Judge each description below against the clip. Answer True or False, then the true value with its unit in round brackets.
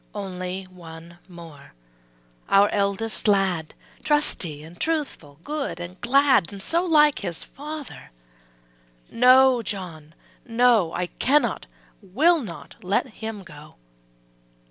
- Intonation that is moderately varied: False (7.2 semitones)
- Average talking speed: False (110 wpm)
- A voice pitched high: True (200 Hz)